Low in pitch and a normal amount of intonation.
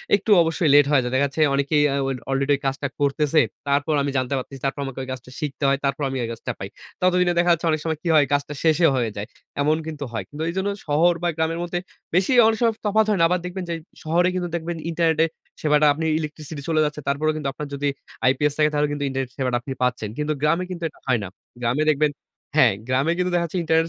No: medium, 150 Hz; average, 3.3 semitones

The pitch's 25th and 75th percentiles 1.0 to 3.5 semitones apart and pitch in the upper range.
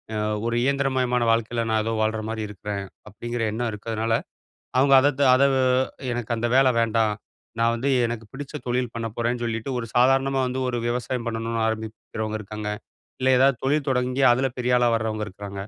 No: narrow, 2.4 semitones; low, 115 Hz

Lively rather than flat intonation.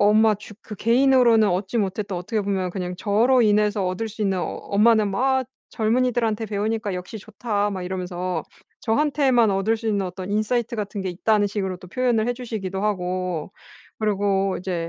No: average, 2.9 semitones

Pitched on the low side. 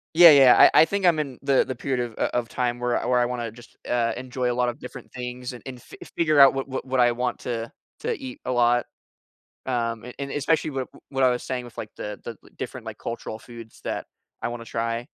Yes: low, 125 Hz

